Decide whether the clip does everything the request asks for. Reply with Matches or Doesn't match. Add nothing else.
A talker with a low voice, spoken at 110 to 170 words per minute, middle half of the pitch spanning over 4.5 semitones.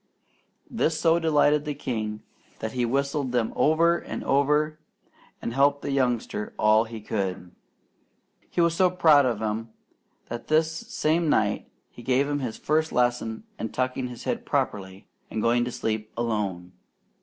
Matches